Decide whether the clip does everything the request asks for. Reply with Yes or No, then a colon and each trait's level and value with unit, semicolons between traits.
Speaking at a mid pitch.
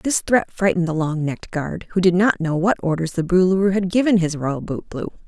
Yes: medium, 180 Hz